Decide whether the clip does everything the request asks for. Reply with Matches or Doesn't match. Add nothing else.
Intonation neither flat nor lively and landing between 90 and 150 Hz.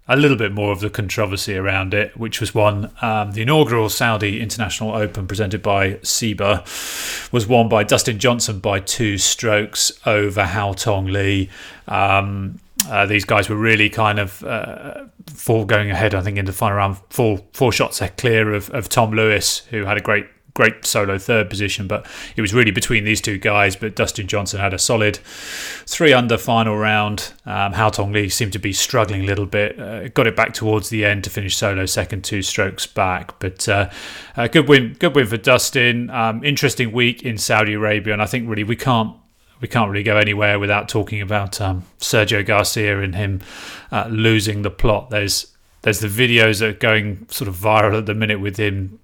Doesn't match